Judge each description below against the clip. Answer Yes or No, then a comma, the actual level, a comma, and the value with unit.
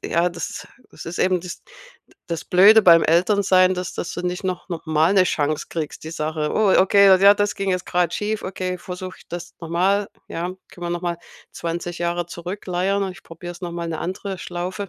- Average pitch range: No, narrow, 1.9 semitones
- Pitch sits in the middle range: Yes, medium, 180 Hz